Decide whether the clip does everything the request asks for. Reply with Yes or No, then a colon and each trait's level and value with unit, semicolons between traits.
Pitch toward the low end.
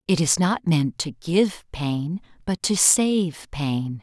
No: medium, 165 Hz